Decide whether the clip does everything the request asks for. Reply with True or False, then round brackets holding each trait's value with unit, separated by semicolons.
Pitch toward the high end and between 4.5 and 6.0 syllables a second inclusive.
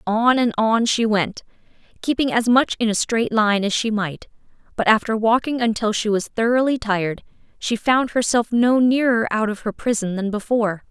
True (225 Hz; 5.0 syllables/s)